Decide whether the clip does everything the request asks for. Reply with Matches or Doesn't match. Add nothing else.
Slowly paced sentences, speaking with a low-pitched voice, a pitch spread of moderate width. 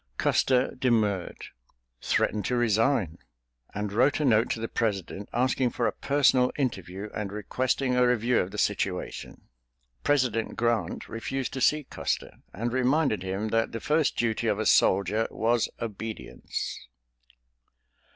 Matches